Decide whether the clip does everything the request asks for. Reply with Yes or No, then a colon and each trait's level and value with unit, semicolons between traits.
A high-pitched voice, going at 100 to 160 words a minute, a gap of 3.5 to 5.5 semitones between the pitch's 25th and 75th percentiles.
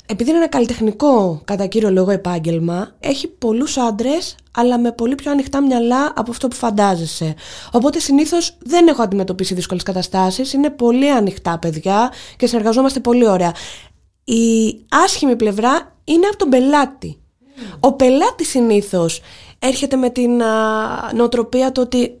Yes: high, 240 Hz; average, 140 wpm; average, 4.9 semitones